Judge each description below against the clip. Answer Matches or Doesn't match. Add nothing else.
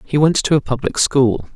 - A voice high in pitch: Doesn't match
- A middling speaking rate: Doesn't match